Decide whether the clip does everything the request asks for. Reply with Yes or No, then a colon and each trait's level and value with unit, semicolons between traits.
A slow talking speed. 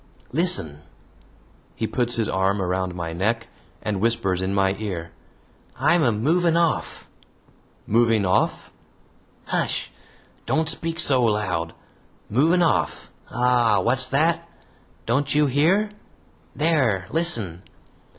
Yes: slow, 110 wpm